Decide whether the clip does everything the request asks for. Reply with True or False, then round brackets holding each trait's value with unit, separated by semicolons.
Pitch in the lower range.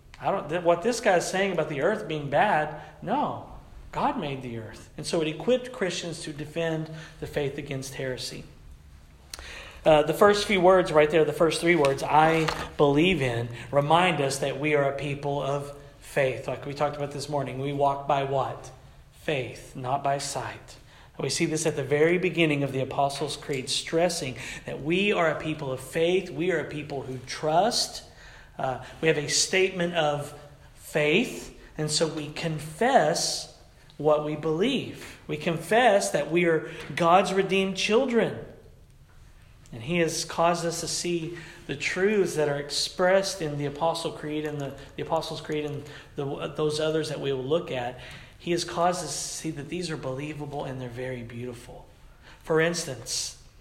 False (150 Hz)